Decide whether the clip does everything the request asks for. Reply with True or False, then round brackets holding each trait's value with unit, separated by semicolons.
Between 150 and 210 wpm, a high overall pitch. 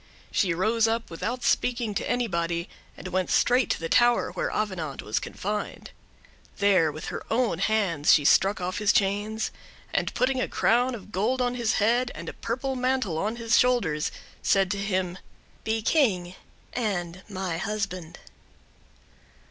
True (155 wpm; 205 Hz)